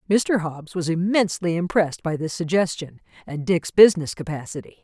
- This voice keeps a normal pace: Yes, average, 150 wpm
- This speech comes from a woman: Yes, female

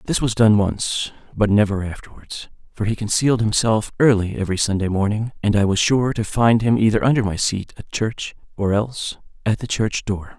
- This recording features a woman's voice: No, male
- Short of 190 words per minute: No, average, 195 wpm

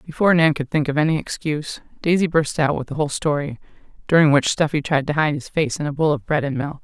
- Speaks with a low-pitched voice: No, medium, 150 Hz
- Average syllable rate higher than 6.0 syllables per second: Yes, 6.5 syllables/s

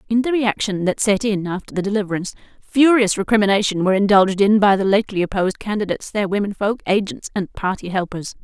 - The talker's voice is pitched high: Yes, high, 200 Hz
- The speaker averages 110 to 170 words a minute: No, average, 185 wpm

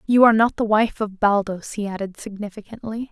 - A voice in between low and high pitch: No, high, 210 Hz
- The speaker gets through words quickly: No, average, 195 wpm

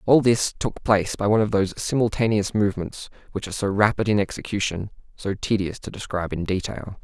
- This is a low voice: Yes, low, 100 Hz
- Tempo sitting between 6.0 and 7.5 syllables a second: Yes, 6.2 syllables/s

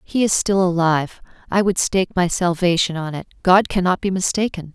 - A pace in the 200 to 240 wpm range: No, average, 190 wpm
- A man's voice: No, female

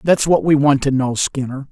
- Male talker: Yes, male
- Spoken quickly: Yes, fast, 245 wpm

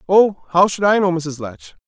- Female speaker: No, male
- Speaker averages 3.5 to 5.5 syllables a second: Yes, 4.5 syllables/s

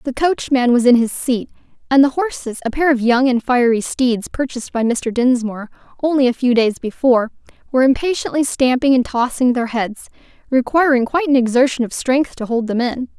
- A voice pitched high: Yes, very high, 255 Hz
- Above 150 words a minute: Yes, average, 190 wpm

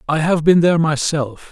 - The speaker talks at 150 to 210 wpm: Yes, average, 200 wpm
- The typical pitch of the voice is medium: Yes, medium, 155 Hz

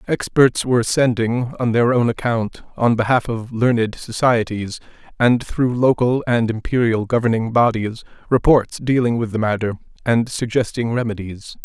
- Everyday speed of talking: No, slow, 130 wpm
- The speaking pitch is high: No, low, 115 Hz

